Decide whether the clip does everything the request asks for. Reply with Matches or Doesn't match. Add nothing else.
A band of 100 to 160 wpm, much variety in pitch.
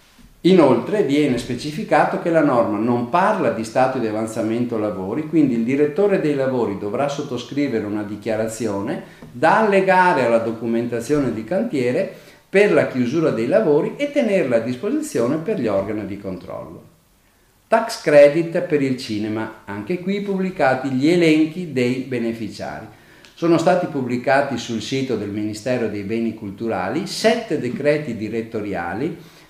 Matches